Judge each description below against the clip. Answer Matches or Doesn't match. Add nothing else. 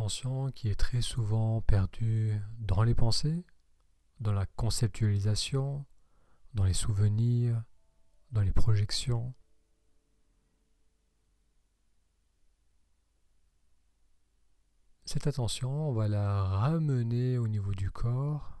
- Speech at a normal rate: Doesn't match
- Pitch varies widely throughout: Matches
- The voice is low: Matches